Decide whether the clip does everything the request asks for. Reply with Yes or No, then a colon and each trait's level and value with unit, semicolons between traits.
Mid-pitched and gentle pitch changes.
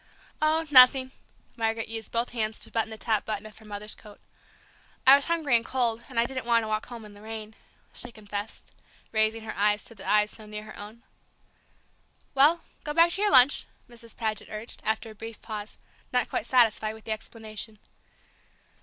No: high, 225 Hz; narrow, 2.2 semitones